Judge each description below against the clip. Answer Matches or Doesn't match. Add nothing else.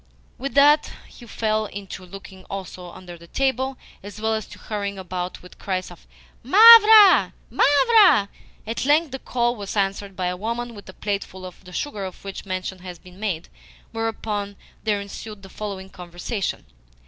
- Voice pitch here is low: Doesn't match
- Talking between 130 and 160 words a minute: Doesn't match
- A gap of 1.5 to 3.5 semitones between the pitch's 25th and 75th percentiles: Doesn't match